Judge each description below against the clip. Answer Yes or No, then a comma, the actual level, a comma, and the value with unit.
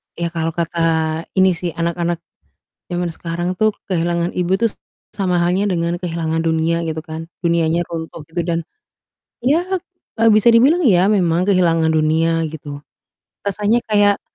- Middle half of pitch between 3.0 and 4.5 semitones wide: No, narrow, 2.4 semitones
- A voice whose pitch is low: No, medium, 170 Hz